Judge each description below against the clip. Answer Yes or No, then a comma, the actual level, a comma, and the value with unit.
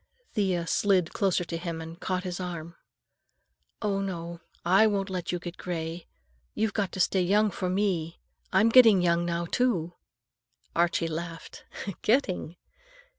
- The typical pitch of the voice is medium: Yes, medium, 180 Hz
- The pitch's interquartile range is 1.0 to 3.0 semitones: Yes, narrow, 2.5 semitones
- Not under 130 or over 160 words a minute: Yes, average, 145 wpm